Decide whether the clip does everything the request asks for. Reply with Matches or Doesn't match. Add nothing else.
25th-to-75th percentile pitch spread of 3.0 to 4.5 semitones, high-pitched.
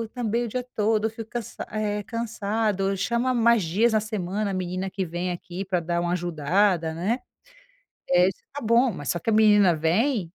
Matches